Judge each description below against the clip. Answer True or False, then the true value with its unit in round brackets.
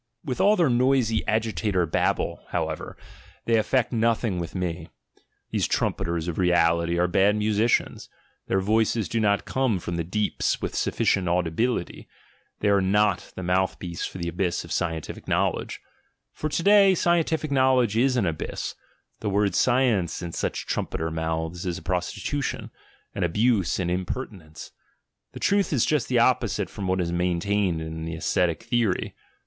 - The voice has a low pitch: True (100 Hz)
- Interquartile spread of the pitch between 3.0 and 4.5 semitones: False (5.4 semitones)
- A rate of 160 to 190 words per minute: True (165 wpm)